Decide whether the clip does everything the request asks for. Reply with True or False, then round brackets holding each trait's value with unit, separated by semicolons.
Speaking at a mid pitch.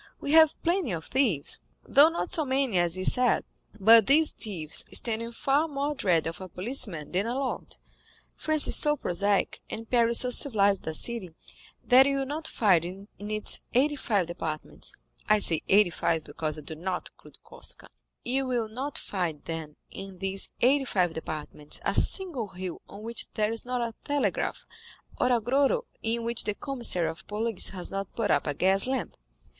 False (220 Hz)